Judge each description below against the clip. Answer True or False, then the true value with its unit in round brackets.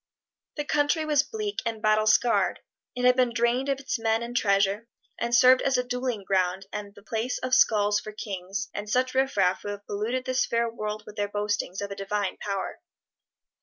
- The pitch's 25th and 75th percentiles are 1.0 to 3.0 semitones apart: False (3.7 semitones)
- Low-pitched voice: False (225 Hz)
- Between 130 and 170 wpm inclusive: False (200 wpm)